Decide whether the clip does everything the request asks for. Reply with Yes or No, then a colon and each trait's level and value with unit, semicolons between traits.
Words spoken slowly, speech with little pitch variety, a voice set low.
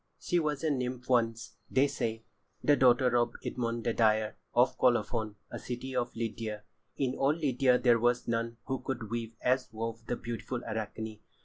No: average, 170 wpm; narrow, 2.0 semitones; low, 120 Hz